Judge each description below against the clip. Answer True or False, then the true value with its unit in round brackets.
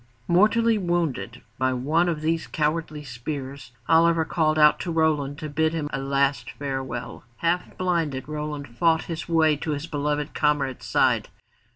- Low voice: False (150 Hz)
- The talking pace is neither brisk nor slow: True (155 wpm)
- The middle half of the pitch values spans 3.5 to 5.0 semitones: False (2.7 semitones)